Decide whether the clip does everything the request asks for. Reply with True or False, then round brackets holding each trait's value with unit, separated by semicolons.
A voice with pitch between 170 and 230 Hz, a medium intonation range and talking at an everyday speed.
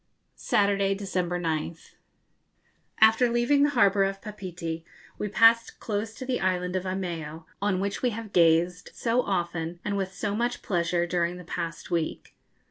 True (190 Hz; 3.5 semitones; 160 wpm)